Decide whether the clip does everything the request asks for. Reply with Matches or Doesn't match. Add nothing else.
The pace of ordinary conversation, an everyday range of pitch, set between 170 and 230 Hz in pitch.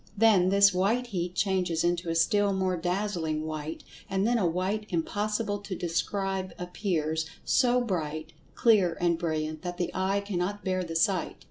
Matches